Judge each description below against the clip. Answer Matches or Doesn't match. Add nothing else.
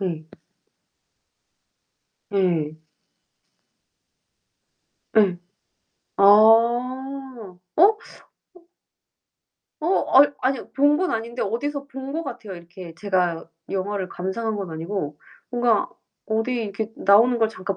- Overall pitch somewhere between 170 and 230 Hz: Matches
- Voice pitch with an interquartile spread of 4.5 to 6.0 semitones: Matches